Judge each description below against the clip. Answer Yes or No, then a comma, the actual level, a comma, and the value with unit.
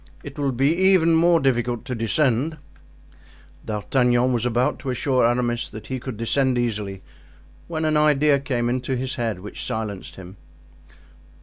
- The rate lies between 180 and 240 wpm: No, average, 150 wpm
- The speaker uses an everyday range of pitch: Yes, average, 3.3 semitones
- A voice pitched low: Yes, low, 125 Hz